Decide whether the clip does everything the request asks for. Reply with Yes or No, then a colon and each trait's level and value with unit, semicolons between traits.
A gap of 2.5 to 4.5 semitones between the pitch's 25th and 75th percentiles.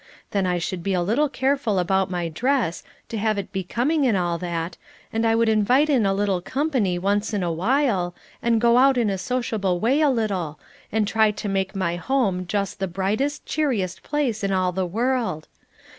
No: average, 5.1 semitones